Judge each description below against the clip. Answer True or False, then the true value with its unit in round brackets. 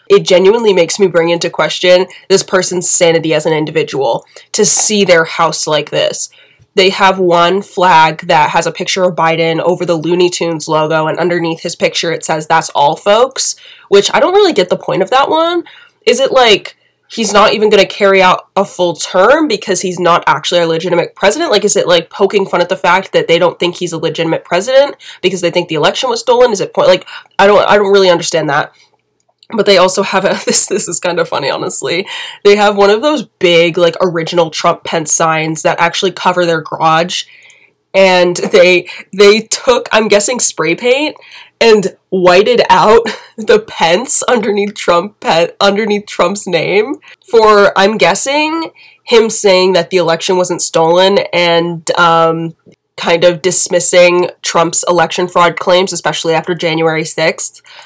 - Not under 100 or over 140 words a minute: False (185 wpm)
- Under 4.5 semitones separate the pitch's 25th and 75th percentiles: True (3.4 semitones)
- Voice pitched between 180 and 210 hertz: True (185 Hz)